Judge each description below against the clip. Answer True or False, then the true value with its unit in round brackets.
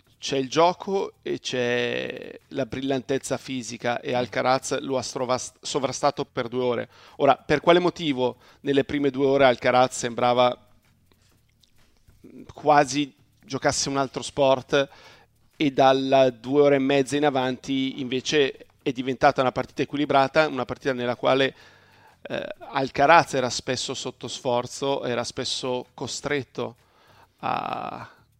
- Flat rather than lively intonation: True (2.3 semitones)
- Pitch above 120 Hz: True (130 Hz)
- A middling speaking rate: True (125 wpm)